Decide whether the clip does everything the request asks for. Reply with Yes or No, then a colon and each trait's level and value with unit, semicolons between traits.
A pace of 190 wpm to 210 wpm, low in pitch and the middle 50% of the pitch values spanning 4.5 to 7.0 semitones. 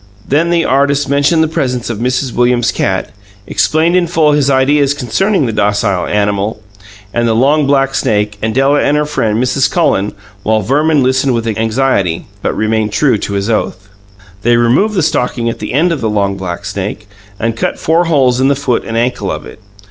Yes: average, 195 wpm; low, 125 Hz; average, 4.8 semitones